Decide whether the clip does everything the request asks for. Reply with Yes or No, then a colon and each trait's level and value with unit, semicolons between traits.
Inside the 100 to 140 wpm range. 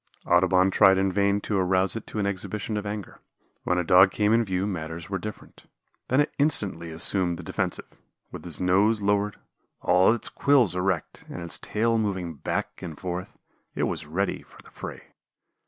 No: average, 185 wpm